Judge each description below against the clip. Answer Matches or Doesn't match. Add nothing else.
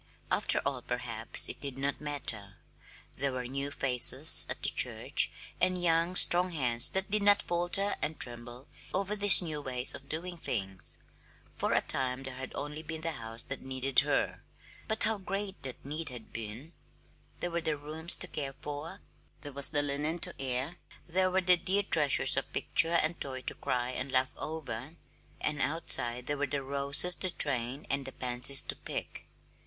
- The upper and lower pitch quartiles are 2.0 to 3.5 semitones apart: Doesn't match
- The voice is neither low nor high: Matches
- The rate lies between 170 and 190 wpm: Matches